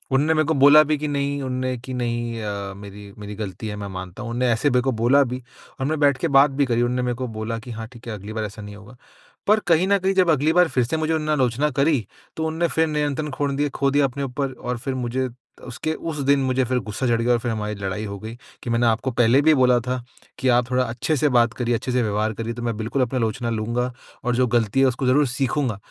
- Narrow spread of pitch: No, average, 3.6 semitones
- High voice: No, low, 125 Hz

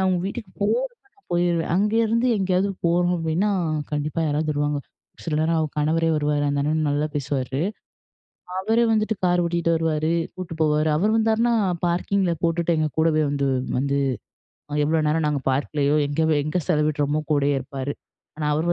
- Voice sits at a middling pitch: Yes, medium, 160 Hz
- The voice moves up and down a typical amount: Yes, average, 3.4 semitones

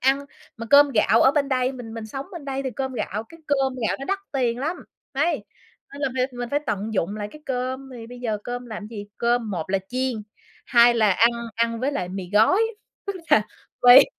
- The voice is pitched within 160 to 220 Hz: No, high, 245 Hz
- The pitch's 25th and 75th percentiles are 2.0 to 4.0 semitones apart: Yes, average, 3.5 semitones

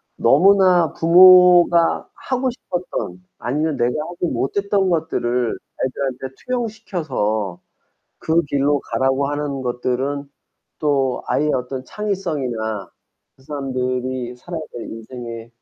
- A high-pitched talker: No, medium, 140 Hz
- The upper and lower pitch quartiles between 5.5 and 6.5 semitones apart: Yes, wide, 5.8 semitones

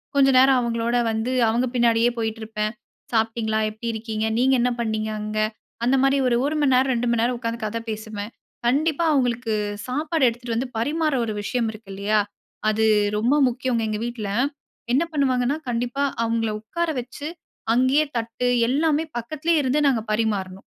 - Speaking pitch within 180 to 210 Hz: No, high, 235 Hz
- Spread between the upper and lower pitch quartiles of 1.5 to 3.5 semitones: Yes, average, 3.0 semitones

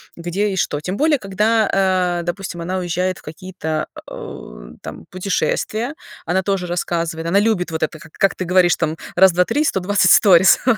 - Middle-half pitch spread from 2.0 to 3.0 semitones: Yes, narrow, 2.5 semitones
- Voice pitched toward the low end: No, medium, 185 Hz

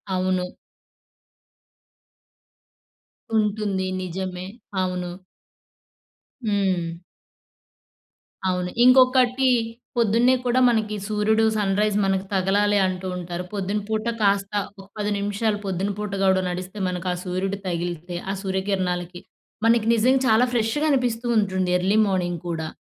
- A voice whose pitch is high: Yes, high, 195 Hz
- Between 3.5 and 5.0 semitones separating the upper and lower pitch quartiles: No, average, 3.0 semitones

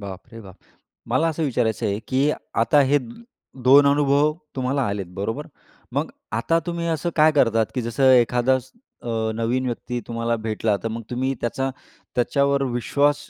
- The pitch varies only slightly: No, average, 3.7 semitones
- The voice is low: Yes, low, 125 Hz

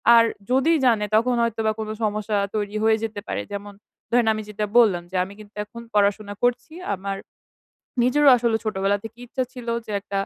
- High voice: Yes, high, 215 Hz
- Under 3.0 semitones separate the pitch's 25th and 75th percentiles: Yes, narrow, 2.5 semitones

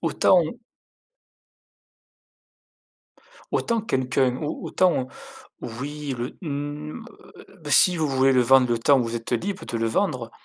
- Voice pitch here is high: No, low, 135 Hz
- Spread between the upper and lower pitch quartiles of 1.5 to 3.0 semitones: No, average, 4.2 semitones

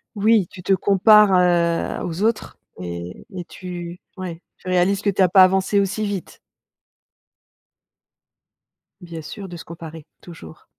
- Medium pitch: Yes, medium, 180 Hz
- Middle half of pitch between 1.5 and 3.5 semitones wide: Yes, narrow, 2.6 semitones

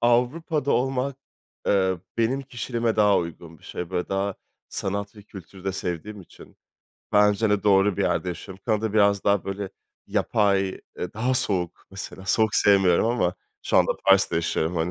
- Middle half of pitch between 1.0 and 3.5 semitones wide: Yes, average, 2.9 semitones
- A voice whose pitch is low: Yes, low, 100 Hz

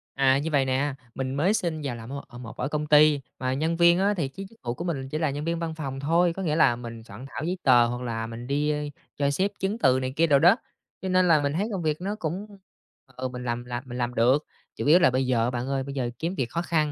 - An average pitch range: Yes, average, 4.7 semitones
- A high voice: No, medium, 140 Hz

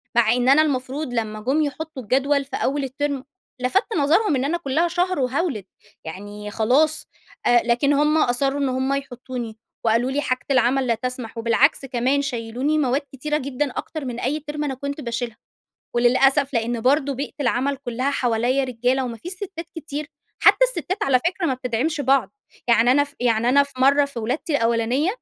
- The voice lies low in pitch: No, very high, 265 Hz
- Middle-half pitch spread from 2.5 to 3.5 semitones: Yes, average, 3.1 semitones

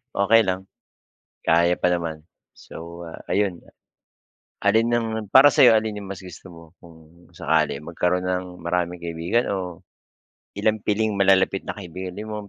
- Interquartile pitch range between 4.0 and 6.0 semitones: No, average, 3.6 semitones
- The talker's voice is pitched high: No, very low, 95 Hz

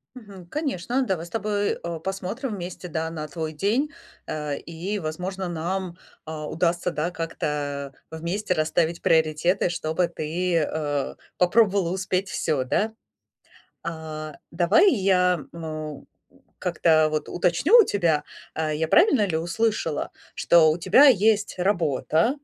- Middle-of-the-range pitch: Yes, medium, 170 Hz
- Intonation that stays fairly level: No, average, 3.6 semitones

